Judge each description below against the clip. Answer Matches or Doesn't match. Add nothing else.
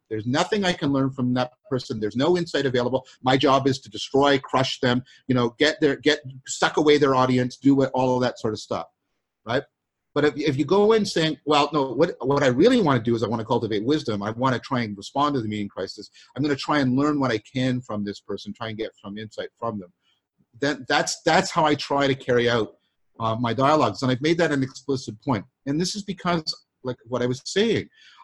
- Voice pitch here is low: Matches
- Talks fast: Matches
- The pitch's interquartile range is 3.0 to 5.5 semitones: Matches